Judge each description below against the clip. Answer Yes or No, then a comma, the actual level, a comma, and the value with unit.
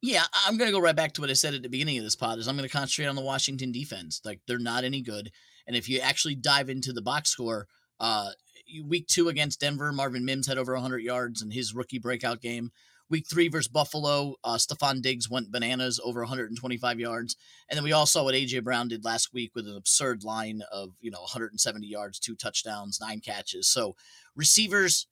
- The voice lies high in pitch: No, low, 130 Hz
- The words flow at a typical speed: No, fast, 220 wpm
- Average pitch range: Yes, average, 3.7 semitones